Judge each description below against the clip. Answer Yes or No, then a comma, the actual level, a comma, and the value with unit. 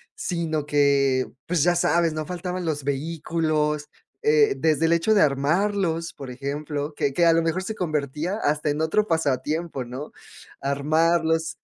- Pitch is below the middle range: No, medium, 160 Hz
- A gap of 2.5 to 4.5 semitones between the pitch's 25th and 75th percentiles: Yes, average, 2.8 semitones